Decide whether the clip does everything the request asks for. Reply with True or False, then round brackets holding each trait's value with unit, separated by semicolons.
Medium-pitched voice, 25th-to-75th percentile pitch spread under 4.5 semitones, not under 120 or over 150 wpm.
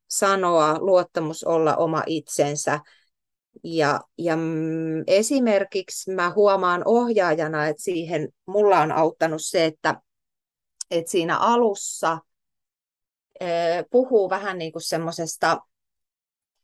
False (170 Hz; 3.4 semitones; 95 wpm)